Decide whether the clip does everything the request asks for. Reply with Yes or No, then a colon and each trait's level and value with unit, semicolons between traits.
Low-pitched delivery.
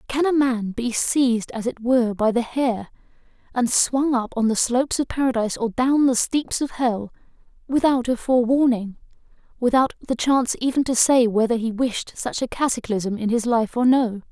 No: high, 245 Hz